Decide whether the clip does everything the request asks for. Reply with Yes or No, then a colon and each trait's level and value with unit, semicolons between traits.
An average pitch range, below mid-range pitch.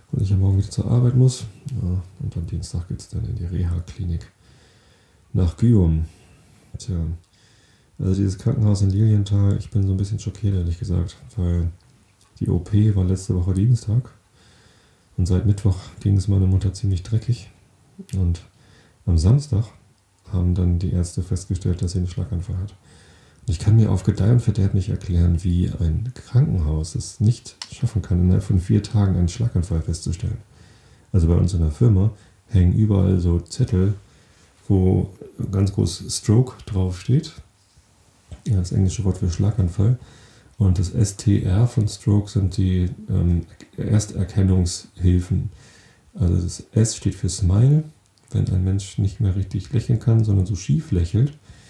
Yes: average, 3.3 semitones; low, 100 Hz